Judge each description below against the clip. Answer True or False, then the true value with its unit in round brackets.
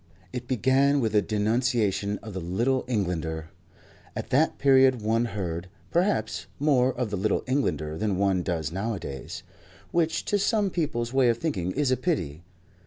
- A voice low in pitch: True (115 Hz)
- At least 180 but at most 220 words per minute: False (160 wpm)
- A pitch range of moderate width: False (5.9 semitones)